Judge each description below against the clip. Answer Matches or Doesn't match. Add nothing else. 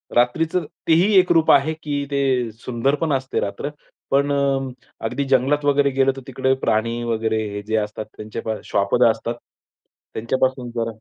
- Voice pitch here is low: Matches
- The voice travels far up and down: Doesn't match